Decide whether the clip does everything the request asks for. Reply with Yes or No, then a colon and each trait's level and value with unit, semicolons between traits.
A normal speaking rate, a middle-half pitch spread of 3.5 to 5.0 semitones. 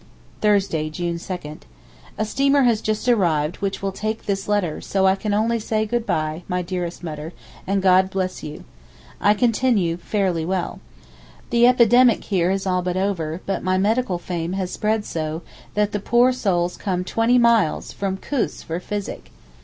Yes: average, 170 wpm; average, 3.8 semitones